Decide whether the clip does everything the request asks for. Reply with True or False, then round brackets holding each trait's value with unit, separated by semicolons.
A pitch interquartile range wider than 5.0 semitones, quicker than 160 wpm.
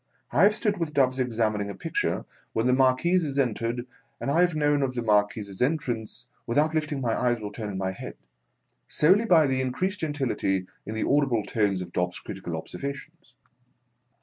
True (5.6 semitones; 175 wpm)